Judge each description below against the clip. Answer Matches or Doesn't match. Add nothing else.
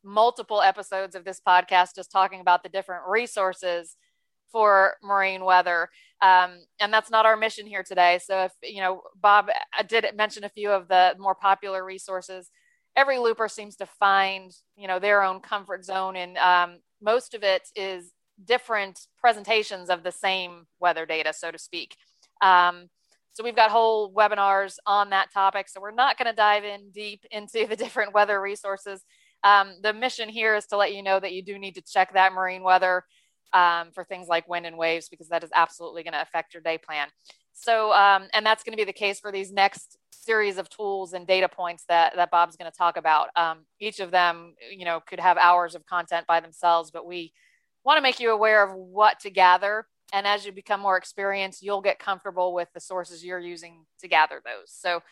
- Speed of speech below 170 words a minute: Doesn't match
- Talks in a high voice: Matches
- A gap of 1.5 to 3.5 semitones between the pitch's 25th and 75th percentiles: Matches